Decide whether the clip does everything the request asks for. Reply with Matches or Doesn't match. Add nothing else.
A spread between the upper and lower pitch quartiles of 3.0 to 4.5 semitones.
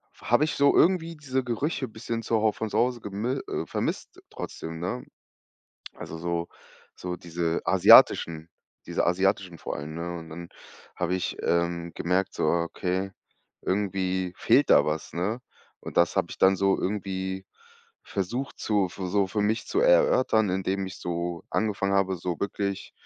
Matches